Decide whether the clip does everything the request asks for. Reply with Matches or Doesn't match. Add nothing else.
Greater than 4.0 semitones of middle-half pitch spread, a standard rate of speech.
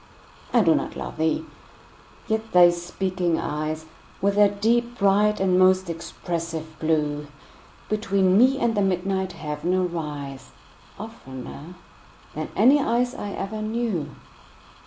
Doesn't match